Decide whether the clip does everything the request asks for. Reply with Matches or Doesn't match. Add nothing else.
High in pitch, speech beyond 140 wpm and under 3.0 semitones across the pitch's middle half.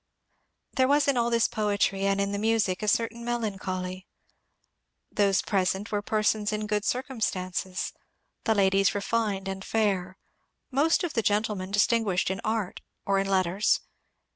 Matches